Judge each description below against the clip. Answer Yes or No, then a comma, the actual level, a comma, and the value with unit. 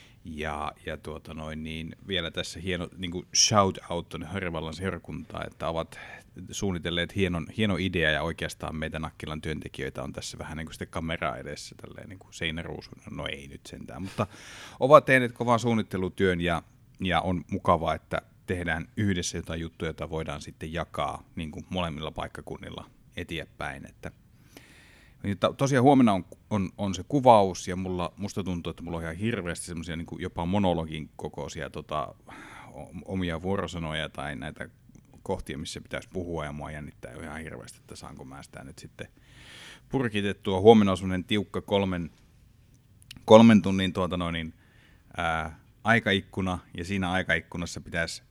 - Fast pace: No, average, 145 wpm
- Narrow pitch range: No, average, 3.4 semitones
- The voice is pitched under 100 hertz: Yes, very low, 90 Hz